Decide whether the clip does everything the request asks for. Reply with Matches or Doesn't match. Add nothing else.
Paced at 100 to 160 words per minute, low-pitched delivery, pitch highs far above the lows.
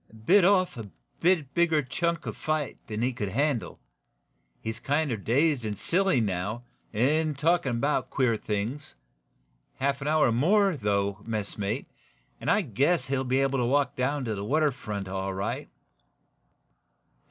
Matches